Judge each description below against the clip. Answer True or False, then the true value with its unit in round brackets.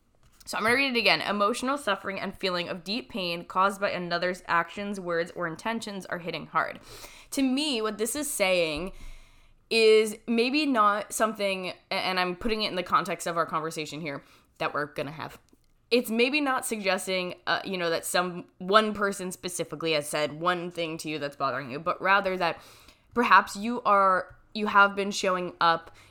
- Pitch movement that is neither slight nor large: True (4.3 semitones)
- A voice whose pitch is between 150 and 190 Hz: True (185 Hz)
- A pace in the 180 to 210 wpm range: True (190 wpm)